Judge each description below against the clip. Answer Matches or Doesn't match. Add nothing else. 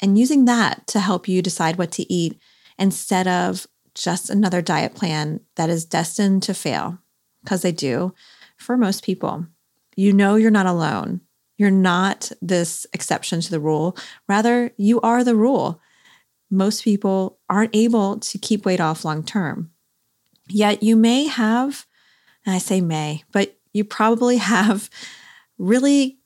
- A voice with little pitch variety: Doesn't match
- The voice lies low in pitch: Doesn't match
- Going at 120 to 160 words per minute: Matches